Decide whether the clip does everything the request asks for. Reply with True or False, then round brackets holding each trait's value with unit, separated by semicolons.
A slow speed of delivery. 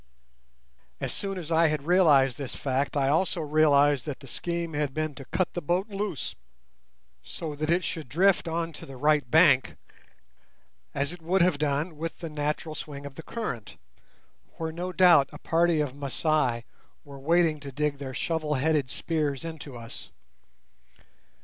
False (170 wpm)